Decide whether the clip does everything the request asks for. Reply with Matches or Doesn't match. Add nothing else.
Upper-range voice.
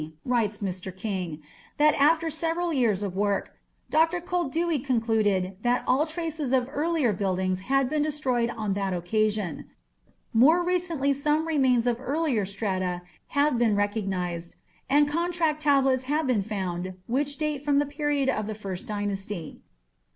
Matches